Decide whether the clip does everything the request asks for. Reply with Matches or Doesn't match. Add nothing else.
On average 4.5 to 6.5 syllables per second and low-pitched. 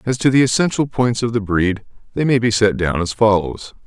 Matches